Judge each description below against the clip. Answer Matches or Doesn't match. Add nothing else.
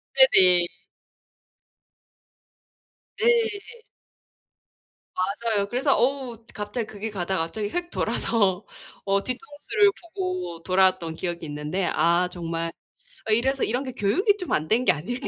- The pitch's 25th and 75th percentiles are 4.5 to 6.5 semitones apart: Doesn't match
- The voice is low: Doesn't match